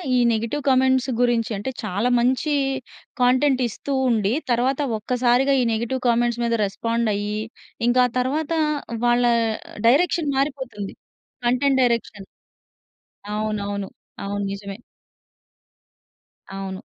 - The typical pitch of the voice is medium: No, high, 240 Hz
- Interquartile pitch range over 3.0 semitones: Yes, average, 3.6 semitones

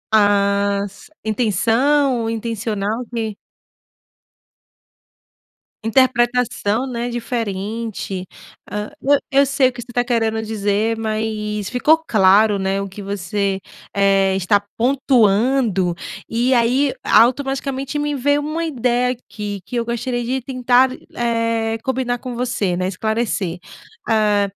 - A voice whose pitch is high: Yes, high, 230 Hz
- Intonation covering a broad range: No, average, 3.5 semitones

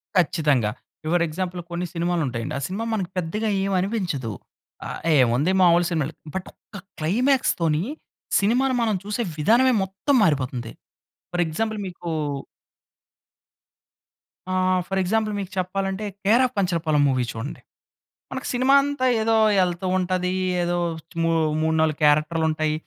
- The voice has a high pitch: No, medium, 180 Hz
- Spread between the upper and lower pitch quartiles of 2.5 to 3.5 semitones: No, average, 4.8 semitones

